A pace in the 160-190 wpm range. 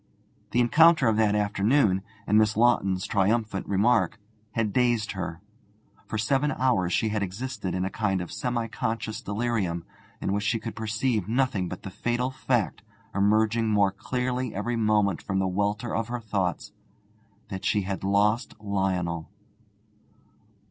No: average, 150 wpm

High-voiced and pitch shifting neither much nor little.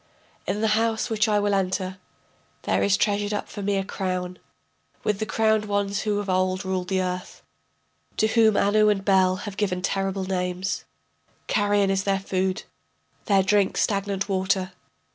No: high, 195 Hz; narrow, 1.6 semitones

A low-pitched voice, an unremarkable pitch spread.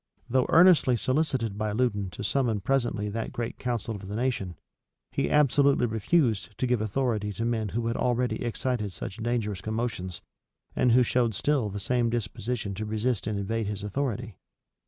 Yes: low, 115 Hz; average, 3.2 semitones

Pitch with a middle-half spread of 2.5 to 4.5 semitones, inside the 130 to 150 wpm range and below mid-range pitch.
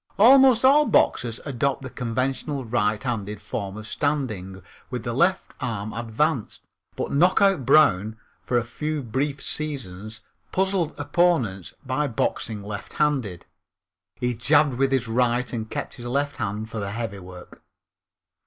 No: average, 5.2 semitones; slow, 135 wpm; low, 125 Hz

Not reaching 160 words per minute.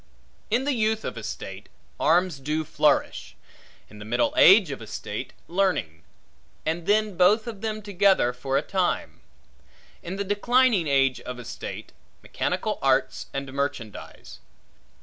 Yes: average, 150 wpm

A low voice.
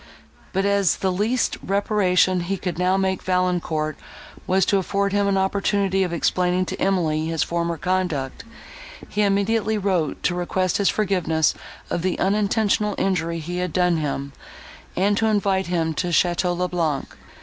No: medium, 185 Hz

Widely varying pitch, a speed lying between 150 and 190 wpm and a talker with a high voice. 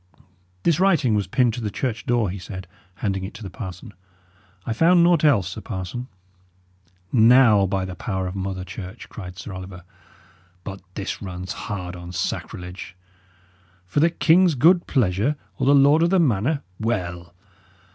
No: wide, 6.2 semitones; average, 165 wpm; low, 105 Hz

